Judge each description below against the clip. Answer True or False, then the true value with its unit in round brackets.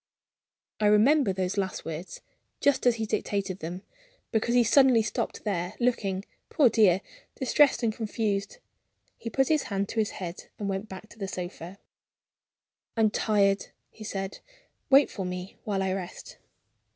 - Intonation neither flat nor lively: True (3.3 semitones)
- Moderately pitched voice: False (205 Hz)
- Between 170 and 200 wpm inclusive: False (155 wpm)